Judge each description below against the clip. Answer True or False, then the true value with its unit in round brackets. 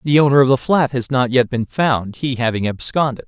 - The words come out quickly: True (240 wpm)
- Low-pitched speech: True (130 Hz)